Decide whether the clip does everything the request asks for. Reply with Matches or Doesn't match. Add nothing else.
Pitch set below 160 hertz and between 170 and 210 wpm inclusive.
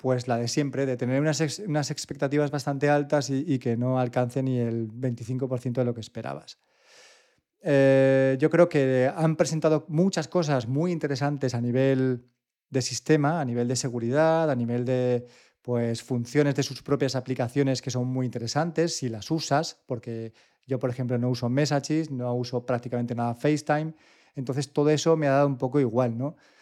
Matches